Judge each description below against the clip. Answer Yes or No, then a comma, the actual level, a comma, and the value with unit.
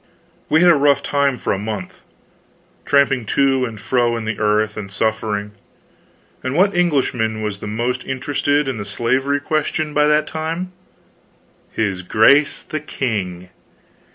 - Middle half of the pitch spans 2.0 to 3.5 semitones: No, average, 5.1 semitones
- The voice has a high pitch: No, low, 125 Hz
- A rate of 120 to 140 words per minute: No, average, 150 wpm